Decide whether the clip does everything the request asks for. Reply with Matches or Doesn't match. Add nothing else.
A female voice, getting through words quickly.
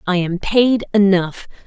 Doesn't match